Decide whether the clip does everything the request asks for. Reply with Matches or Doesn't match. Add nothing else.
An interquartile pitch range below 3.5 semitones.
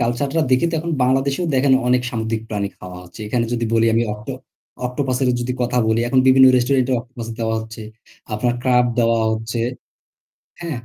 Matches